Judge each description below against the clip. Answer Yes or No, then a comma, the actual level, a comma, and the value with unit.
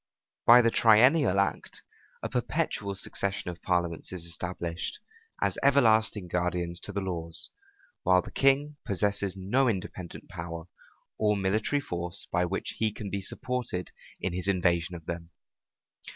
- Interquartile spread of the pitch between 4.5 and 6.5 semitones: No, average, 3.8 semitones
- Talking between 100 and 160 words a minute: Yes, average, 140 wpm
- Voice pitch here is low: Yes, very low, 95 Hz